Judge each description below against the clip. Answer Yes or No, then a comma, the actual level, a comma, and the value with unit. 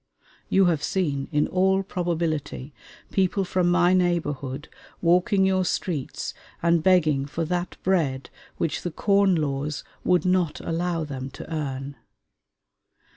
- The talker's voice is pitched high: No, medium, 170 Hz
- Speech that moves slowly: Yes, slow, 130 wpm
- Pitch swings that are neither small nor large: Yes, average, 3.7 semitones